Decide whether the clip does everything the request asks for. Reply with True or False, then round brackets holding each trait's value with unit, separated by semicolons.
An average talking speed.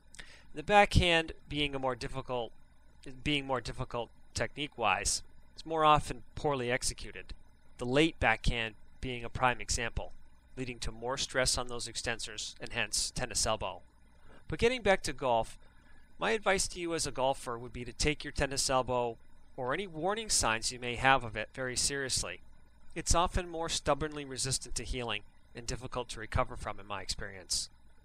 True (170 wpm)